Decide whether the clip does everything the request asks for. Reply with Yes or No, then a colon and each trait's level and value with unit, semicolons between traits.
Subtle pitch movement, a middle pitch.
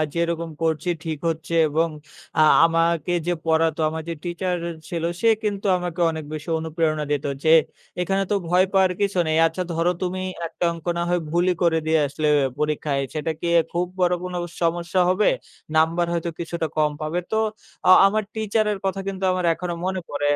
Yes: narrow, 2.2 semitones; medium, 170 Hz